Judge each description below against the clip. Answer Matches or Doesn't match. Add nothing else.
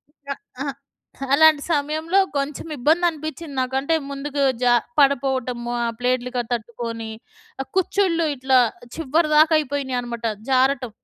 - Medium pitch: Doesn't match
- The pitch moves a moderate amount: Matches